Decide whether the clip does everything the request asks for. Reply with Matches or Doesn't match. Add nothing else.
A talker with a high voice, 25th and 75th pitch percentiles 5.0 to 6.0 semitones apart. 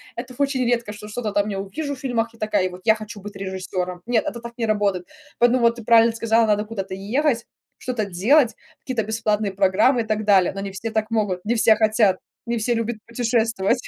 Doesn't match